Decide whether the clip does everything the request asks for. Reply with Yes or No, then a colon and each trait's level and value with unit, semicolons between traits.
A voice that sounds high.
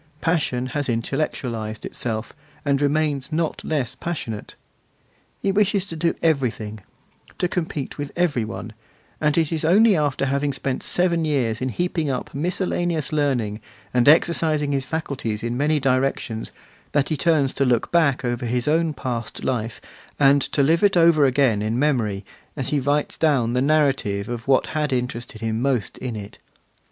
No: medium, 140 Hz